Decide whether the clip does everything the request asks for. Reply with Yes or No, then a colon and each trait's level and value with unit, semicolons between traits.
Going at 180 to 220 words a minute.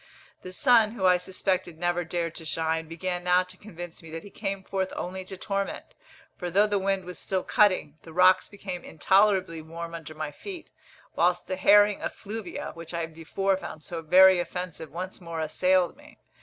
Yes: average, 185 wpm